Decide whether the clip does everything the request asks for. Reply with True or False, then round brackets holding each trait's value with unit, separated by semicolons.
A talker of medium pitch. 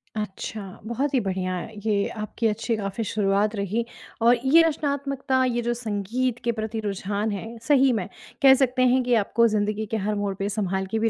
False (220 Hz)